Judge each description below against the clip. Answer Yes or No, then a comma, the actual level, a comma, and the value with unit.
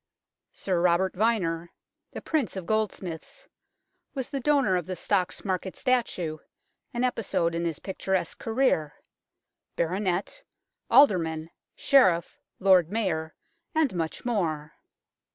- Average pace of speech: No, slow, 115 wpm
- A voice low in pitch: No, medium, 185 Hz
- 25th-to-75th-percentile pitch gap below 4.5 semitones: No, average, 5.2 semitones